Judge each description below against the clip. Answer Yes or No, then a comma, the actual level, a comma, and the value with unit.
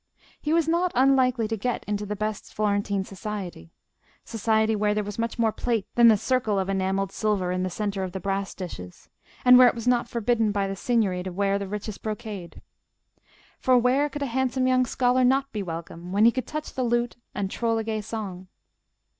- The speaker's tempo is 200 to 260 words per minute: Yes, fast, 205 wpm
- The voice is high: Yes, high, 215 Hz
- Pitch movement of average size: Yes, average, 3.9 semitones